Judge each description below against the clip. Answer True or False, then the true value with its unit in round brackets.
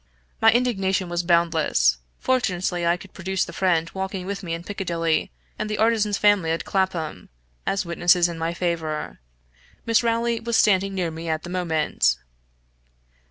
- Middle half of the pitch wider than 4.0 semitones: False (3.1 semitones)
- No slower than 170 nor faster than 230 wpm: False (160 wpm)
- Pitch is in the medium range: True (180 Hz)